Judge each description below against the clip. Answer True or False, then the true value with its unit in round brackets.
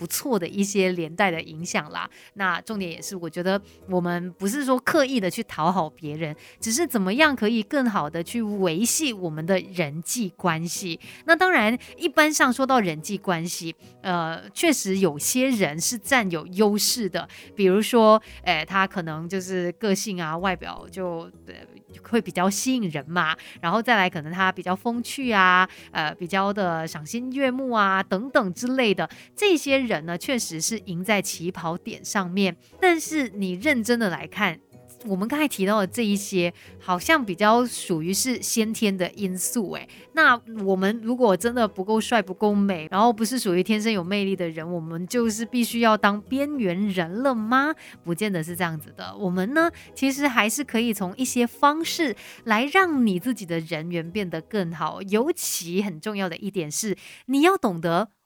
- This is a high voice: True (200 Hz)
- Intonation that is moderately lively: True (5.0 semitones)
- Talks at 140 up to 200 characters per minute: False (265 characters per minute)